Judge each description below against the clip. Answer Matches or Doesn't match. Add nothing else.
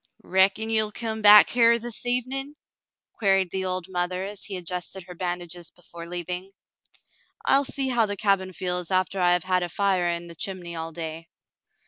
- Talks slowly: Doesn't match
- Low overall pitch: Doesn't match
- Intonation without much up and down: Doesn't match